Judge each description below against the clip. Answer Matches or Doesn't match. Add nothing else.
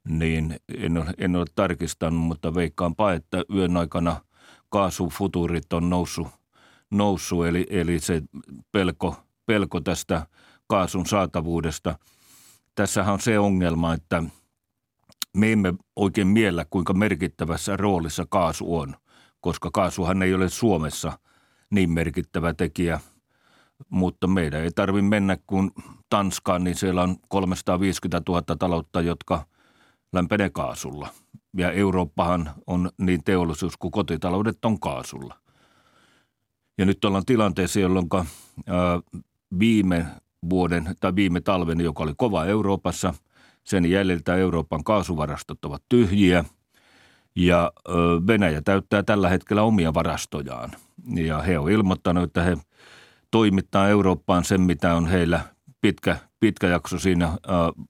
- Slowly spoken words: Doesn't match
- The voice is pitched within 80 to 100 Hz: Matches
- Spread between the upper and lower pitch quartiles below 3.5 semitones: Matches